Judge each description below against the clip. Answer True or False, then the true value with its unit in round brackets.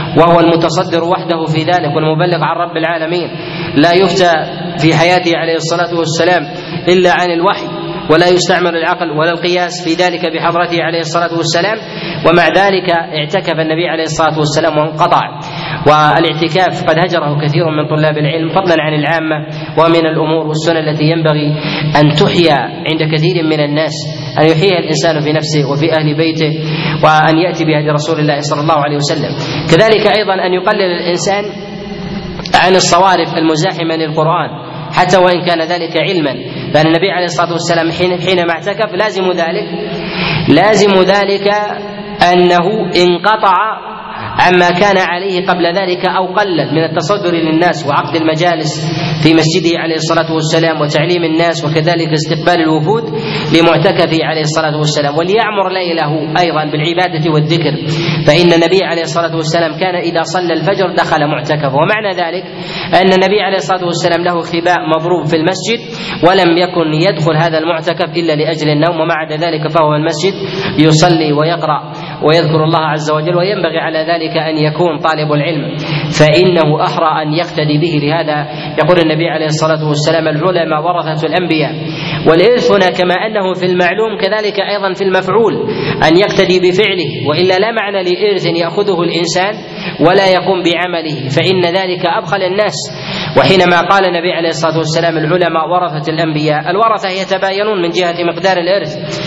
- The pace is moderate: False (145 wpm)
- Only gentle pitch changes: True (2.3 semitones)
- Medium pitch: True (170 Hz)